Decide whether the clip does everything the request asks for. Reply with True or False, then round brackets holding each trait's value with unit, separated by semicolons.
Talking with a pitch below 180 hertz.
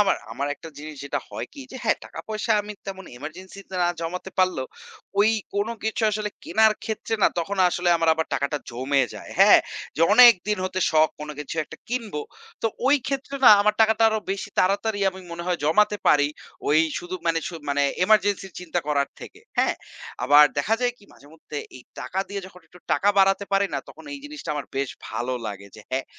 False (185 Hz)